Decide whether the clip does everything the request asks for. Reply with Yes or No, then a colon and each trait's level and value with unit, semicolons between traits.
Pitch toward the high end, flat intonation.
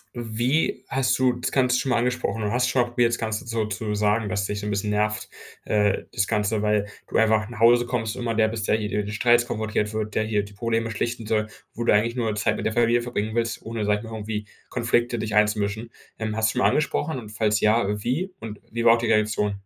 No: low, 110 Hz; narrow, 2.0 semitones